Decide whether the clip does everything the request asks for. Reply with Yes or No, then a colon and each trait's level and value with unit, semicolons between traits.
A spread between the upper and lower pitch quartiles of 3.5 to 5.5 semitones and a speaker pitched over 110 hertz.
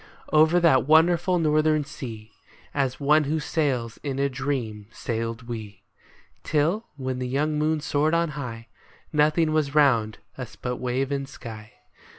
Yes: average, 3.9 semitones; medium, 140 Hz